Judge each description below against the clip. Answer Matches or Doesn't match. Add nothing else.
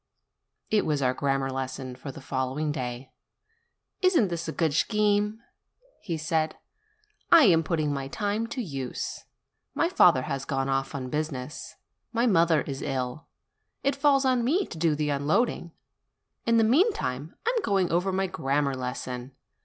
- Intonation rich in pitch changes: Matches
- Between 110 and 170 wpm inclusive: Matches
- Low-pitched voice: Doesn't match